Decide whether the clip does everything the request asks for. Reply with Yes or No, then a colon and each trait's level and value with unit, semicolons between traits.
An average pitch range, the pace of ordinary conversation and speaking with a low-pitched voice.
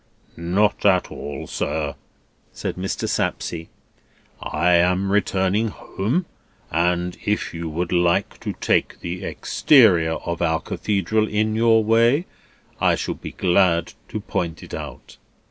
No: average, 3.8 semitones; slow, 130 wpm; very low, 95 Hz